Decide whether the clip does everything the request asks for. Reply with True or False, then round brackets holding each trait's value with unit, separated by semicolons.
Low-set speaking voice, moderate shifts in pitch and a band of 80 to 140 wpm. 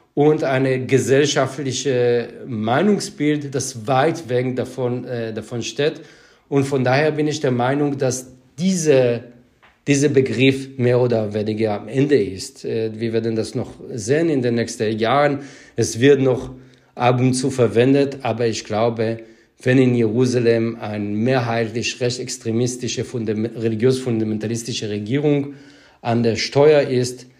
True (125 Hz; 3.0 semitones; 130 wpm)